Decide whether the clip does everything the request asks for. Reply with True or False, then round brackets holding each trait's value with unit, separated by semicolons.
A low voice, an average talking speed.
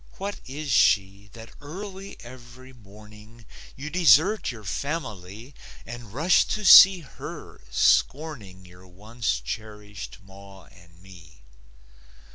False (115 Hz; 110 wpm)